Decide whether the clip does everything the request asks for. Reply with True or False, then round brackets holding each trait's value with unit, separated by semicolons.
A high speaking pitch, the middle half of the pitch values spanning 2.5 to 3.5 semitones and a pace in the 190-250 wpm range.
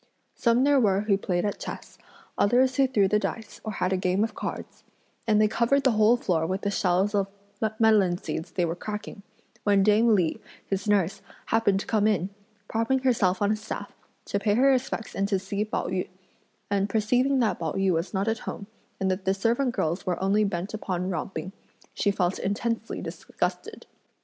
True (205 Hz; 2.8 semitones; 195 wpm)